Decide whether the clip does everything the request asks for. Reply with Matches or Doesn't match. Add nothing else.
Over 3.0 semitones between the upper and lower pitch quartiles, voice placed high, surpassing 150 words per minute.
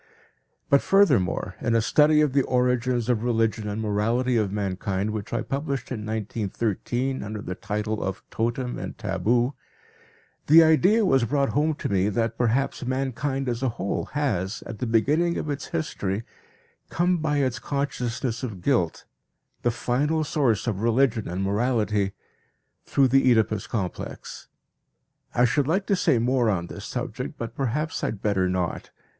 Doesn't match